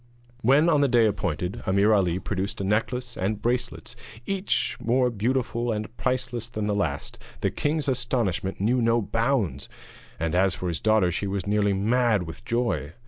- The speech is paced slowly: No, average, 170 wpm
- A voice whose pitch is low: Yes, low, 110 Hz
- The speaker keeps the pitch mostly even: No, average, 4.3 semitones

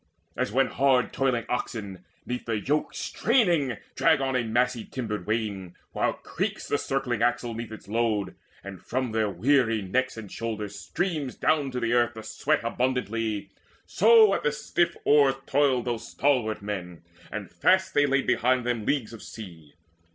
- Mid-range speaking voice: No, low, 120 Hz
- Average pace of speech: Yes, average, 165 wpm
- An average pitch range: Yes, average, 3.9 semitones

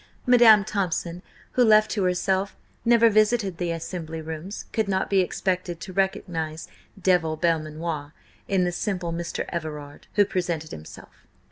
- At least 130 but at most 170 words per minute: Yes, average, 140 wpm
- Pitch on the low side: No, medium, 180 Hz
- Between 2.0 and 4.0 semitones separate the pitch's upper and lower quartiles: Yes, average, 3.4 semitones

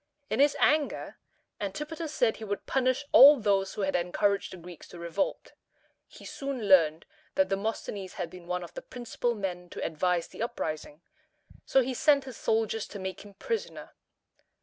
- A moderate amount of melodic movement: No, wide, 6.3 semitones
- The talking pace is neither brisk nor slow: Yes, average, 170 wpm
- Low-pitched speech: No, high, 205 Hz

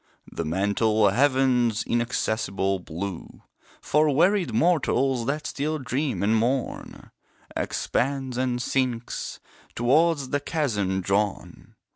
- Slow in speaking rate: Yes, slow, 100 wpm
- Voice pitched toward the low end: Yes, low, 125 Hz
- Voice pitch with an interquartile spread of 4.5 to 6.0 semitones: Yes, average, 4.9 semitones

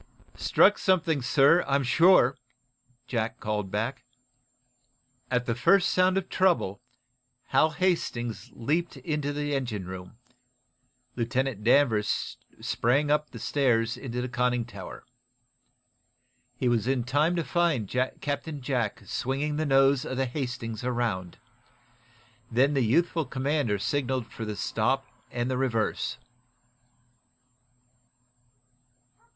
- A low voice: Yes, low, 130 Hz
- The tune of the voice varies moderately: Yes, average, 3.9 semitones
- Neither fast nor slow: No, slow, 115 wpm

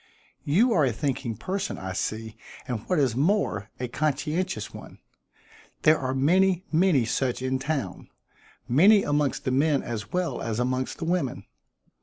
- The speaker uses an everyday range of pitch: No, wide, 5.7 semitones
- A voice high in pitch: No, medium, 140 Hz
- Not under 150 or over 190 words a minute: Yes, average, 155 wpm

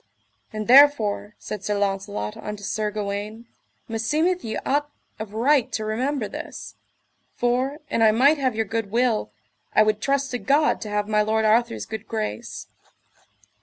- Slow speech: No, average, 160 wpm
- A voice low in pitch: No, high, 220 Hz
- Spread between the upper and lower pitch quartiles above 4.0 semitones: No, average, 3.5 semitones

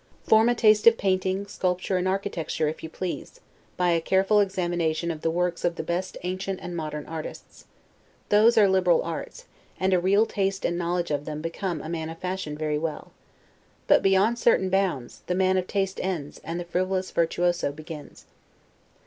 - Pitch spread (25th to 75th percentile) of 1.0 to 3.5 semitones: Yes, average, 2.7 semitones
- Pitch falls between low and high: Yes, medium, 180 Hz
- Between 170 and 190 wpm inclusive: Yes, average, 185 wpm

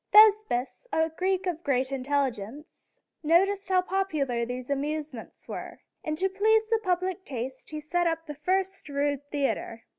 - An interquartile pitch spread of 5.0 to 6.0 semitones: Yes, wide, 5.6 semitones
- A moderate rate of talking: Yes, average, 150 wpm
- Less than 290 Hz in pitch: No, very high, 310 Hz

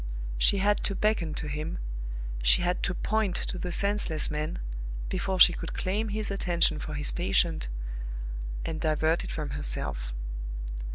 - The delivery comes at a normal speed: Yes, average, 155 wpm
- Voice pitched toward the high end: No, medium, 175 Hz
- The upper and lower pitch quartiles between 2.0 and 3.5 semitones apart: No, average, 4.5 semitones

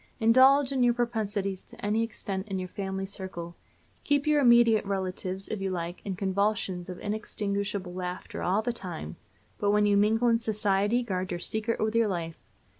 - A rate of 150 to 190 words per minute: Yes, average, 180 wpm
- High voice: Yes, high, 200 Hz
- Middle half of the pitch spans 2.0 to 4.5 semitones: Yes, average, 3.1 semitones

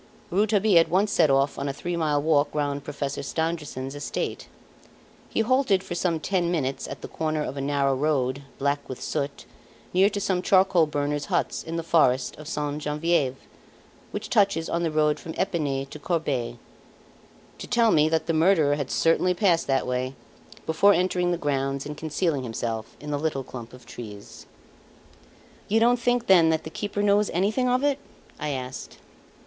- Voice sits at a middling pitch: Yes, medium, 155 Hz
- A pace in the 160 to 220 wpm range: Yes, average, 180 wpm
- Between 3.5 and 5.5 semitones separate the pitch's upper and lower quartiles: Yes, average, 4.6 semitones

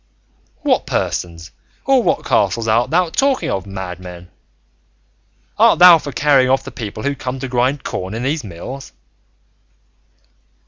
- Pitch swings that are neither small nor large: No, wide, 6.9 semitones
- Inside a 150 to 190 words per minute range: No, average, 140 wpm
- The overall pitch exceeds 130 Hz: No, low, 125 Hz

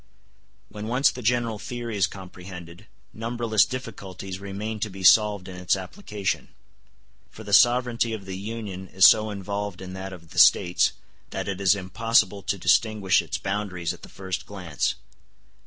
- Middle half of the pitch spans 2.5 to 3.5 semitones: Yes, average, 2.8 semitones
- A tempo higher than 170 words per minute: No, average, 160 wpm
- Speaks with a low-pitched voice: Yes, low, 100 Hz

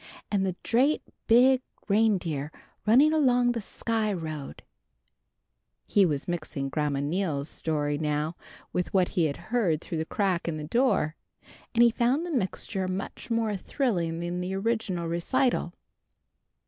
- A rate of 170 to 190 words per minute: No, average, 145 wpm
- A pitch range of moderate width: No, wide, 6.4 semitones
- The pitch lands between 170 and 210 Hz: Yes, medium, 185 Hz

